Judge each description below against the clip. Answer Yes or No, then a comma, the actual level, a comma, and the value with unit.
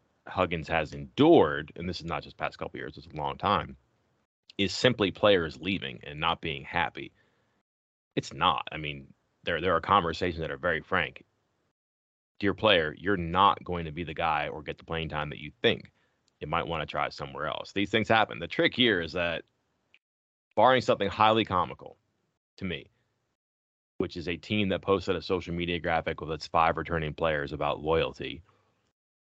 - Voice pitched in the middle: No, very low, 80 Hz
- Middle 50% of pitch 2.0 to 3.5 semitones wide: No, average, 4.2 semitones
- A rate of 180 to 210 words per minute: Yes, average, 185 wpm